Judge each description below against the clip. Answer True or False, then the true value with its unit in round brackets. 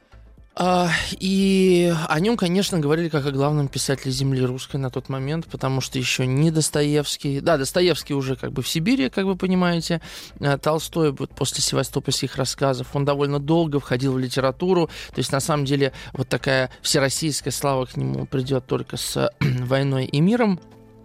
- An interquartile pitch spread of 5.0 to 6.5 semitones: False (3.8 semitones)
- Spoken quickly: True (165 wpm)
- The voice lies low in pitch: False (145 Hz)